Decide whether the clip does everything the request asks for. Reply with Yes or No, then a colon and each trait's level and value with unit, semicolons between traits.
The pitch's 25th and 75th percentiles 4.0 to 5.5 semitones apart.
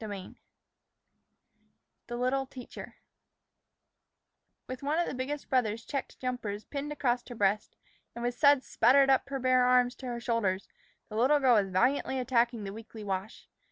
No: average, 3.3 semitones